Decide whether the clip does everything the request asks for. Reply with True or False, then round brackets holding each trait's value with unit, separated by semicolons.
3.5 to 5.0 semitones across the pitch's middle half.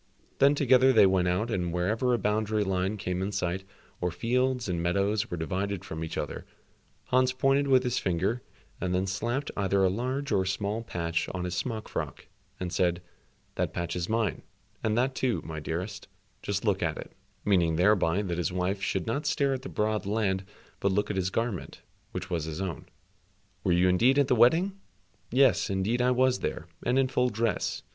False (5.4 semitones)